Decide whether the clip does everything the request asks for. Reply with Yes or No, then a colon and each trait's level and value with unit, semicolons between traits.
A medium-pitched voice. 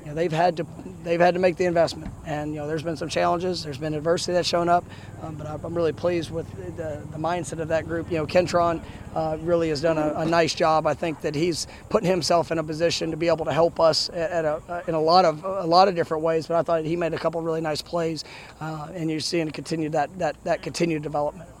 Yes: medium, 165 Hz